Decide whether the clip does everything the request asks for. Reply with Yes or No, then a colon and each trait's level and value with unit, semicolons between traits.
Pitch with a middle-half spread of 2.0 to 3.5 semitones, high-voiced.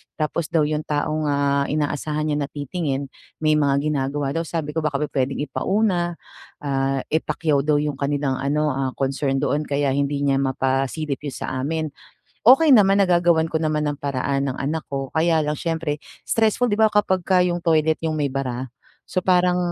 No: average, 2.8 semitones; medium, 150 Hz